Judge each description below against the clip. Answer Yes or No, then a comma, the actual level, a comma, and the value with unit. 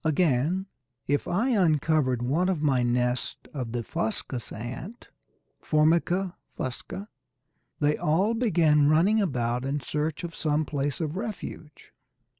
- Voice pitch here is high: No, medium, 150 Hz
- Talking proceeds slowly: Yes, slow, 125 wpm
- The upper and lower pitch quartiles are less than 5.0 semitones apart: No, average, 5.3 semitones